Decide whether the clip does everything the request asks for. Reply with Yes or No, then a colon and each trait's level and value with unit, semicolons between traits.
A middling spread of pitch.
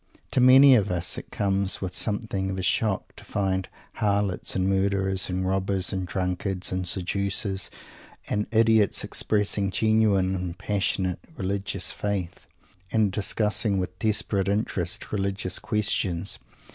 No: narrow, 1.9 semitones